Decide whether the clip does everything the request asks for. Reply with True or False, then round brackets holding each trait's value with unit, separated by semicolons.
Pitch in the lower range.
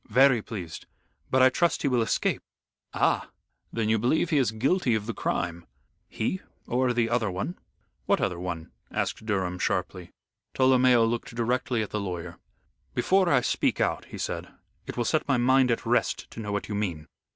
True (115 Hz)